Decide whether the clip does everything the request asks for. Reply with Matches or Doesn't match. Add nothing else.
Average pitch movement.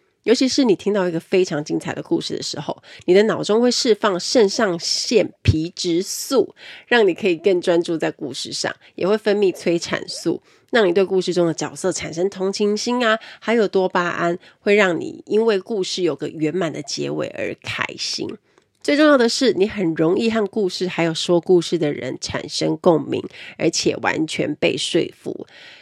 Matches